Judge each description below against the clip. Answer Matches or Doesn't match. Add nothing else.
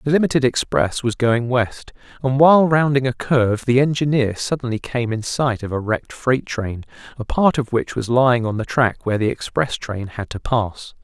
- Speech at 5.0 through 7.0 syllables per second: Matches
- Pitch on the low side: Matches